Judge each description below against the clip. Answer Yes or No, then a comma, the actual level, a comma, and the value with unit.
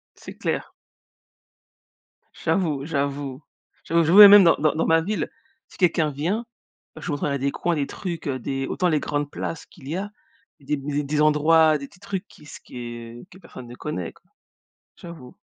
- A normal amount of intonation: Yes, average, 3.4 semitones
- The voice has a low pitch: No, medium, 150 Hz